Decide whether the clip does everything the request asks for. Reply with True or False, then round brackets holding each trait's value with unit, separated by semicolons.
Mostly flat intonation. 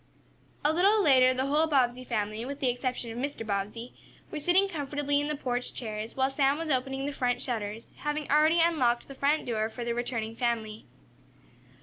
False (3.7 semitones)